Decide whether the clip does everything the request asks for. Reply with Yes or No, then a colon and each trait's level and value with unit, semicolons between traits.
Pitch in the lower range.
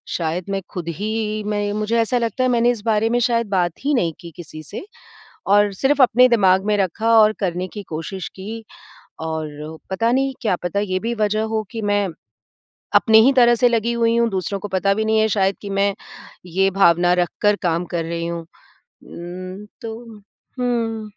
No: high, 205 Hz